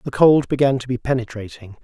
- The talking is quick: No, average, 195 wpm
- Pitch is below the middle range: Yes, low, 125 Hz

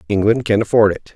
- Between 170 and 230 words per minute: Yes, fast, 205 wpm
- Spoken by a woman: No, male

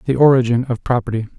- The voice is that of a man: Yes, male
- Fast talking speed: No, average, 175 wpm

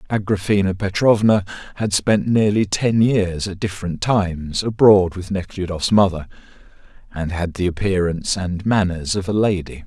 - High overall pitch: No, very low, 95 Hz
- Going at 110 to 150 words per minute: Yes, average, 140 wpm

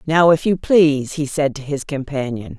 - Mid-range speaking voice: Yes, medium, 145 Hz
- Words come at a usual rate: No, fast, 210 wpm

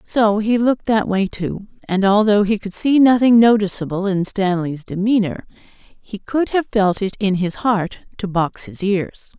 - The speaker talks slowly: No, average, 180 wpm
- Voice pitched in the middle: No, high, 205 Hz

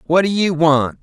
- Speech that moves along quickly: Yes, fast, 235 wpm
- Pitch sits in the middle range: Yes, medium, 165 Hz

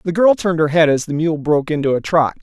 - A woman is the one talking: No, male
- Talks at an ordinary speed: No, fast, 295 wpm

